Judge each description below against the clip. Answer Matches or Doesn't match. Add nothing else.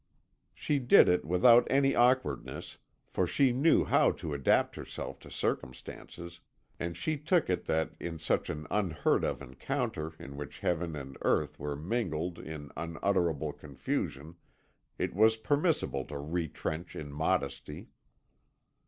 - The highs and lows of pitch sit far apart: Matches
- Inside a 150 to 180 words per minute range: Doesn't match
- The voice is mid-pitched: Doesn't match